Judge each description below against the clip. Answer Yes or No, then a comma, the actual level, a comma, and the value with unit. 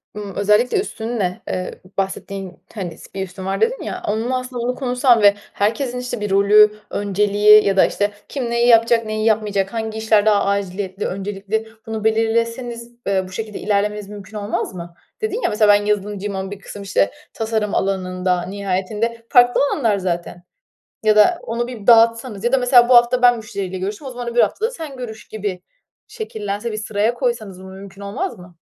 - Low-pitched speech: No, high, 210 Hz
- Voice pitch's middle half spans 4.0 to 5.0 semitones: No, average, 3.1 semitones